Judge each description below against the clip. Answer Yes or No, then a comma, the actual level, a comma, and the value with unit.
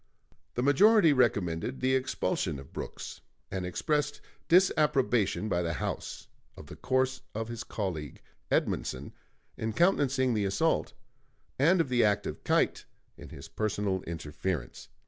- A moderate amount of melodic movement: No, wide, 6.6 semitones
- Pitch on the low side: Yes, low, 115 Hz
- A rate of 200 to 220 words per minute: No, slow, 135 wpm